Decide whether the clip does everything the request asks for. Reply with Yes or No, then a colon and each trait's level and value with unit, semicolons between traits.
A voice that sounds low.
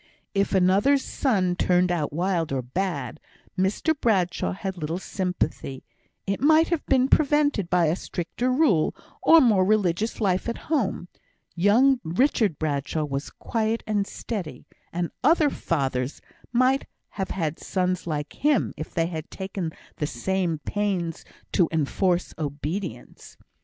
No: medium, 185 Hz